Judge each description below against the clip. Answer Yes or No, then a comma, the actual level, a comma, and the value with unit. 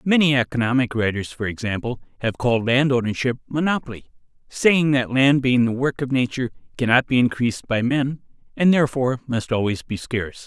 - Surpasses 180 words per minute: No, average, 160 wpm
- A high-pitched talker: No, low, 125 Hz